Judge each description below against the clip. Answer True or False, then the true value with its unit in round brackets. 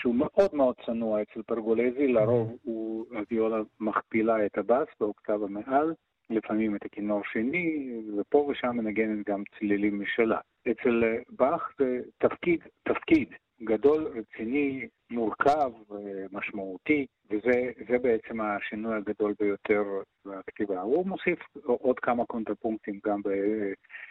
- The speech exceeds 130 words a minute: False (115 wpm)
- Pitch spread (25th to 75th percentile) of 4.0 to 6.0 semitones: False (3.0 semitones)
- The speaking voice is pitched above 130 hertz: False (110 Hz)